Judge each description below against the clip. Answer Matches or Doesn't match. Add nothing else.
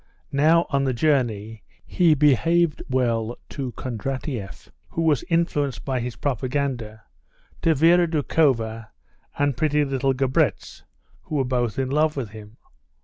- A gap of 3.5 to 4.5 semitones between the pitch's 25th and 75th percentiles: Matches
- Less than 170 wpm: Matches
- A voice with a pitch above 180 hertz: Doesn't match